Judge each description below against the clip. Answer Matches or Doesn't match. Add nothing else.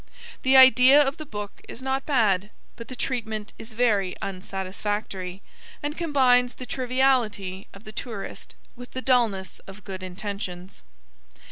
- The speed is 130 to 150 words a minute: Matches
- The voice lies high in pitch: Matches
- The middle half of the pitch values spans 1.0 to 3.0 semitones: Doesn't match